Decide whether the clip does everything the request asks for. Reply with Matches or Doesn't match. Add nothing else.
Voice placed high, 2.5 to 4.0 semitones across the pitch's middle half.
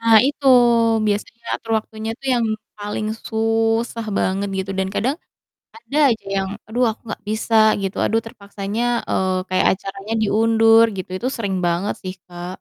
Matches